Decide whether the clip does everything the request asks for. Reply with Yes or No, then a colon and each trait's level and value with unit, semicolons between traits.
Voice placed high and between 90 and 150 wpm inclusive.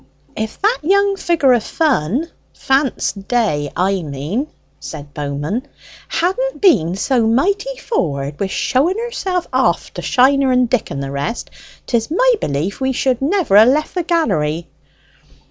Yes: very high, 250 Hz; average, 145 wpm